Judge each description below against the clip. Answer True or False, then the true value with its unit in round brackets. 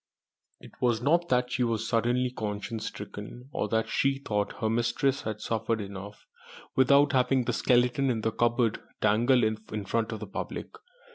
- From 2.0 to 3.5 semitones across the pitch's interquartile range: True (2.6 semitones)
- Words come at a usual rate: True (165 wpm)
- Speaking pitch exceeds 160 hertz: False (115 Hz)